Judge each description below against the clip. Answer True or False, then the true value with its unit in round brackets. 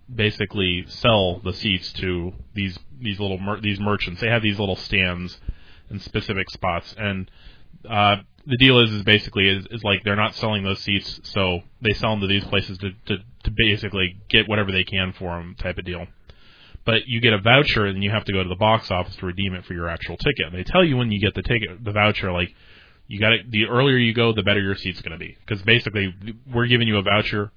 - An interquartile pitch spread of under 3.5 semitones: True (2.7 semitones)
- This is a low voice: True (100 Hz)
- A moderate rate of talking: False (235 wpm)